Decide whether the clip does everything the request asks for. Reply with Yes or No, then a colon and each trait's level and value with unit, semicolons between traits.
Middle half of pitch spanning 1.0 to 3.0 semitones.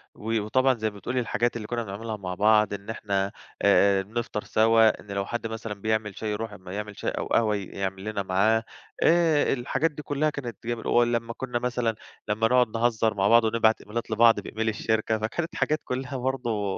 Yes: narrow, 2.4 semitones